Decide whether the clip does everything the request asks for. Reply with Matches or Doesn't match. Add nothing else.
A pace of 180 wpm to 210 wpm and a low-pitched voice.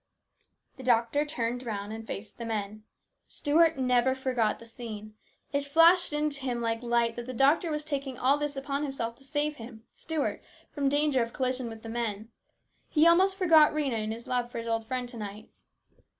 Doesn't match